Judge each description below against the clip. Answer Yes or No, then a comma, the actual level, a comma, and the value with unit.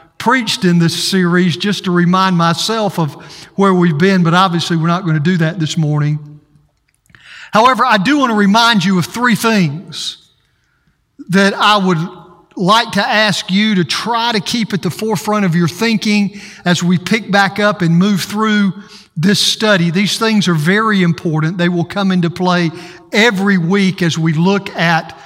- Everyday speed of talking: Yes, average, 180 wpm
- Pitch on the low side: No, medium, 185 Hz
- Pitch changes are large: No, average, 3.6 semitones